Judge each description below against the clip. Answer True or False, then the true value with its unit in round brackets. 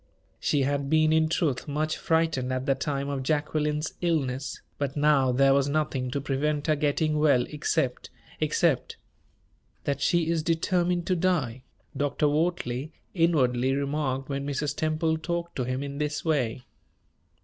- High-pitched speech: False (145 Hz)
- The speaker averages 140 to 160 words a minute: True (150 wpm)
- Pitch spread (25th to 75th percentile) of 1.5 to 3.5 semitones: True (2.6 semitones)